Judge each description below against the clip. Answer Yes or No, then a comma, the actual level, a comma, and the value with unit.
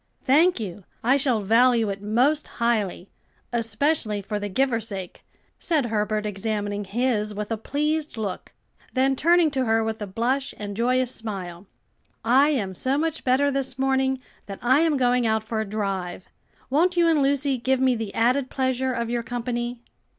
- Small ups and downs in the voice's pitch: No, average, 4.1 semitones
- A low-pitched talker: No, high, 240 Hz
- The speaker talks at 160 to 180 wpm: Yes, average, 170 wpm